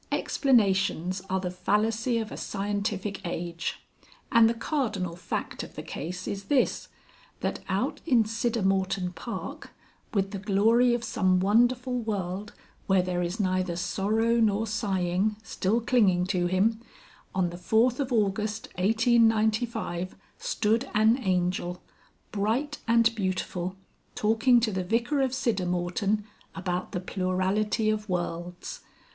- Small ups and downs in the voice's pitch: No, average, 3.6 semitones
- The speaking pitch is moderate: No, high, 205 Hz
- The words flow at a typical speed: No, slow, 130 wpm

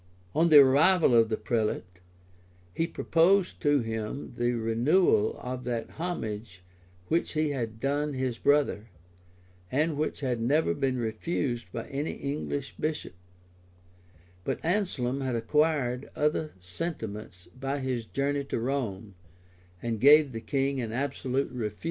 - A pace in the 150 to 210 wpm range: No, slow, 135 wpm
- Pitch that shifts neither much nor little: Yes, average, 4.6 semitones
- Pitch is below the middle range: Yes, low, 130 Hz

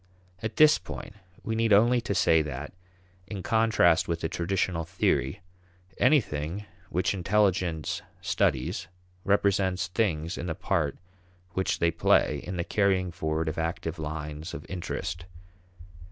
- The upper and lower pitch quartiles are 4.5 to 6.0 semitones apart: No, average, 3.7 semitones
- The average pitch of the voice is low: Yes, very low, 90 Hz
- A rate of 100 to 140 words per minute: Yes, slow, 135 wpm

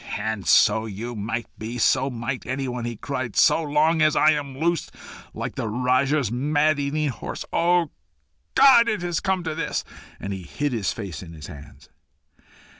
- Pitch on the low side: Yes, low, 130 Hz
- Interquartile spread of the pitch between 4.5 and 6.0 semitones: Yes, wide, 5.4 semitones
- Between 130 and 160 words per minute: No, average, 175 wpm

